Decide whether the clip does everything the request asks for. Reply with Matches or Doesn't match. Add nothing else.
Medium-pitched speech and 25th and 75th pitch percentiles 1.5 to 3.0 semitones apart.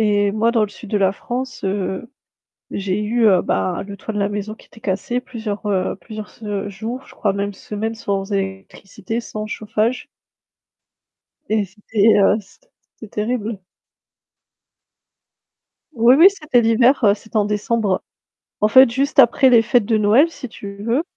Doesn't match